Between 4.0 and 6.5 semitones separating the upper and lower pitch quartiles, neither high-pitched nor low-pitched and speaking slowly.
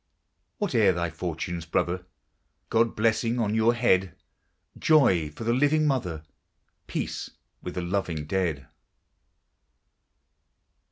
No: wide, 5.4 semitones; very low, 95 Hz; slow, 105 wpm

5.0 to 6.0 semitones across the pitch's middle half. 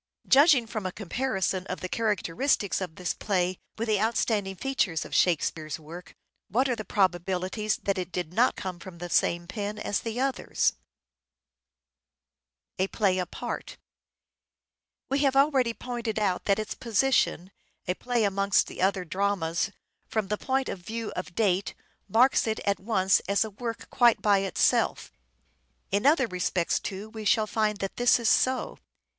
No: average, 3.8 semitones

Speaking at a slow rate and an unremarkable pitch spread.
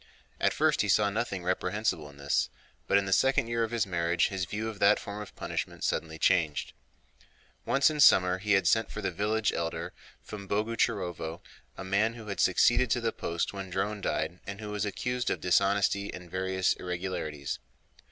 No: average, 190 wpm; average, 3.1 semitones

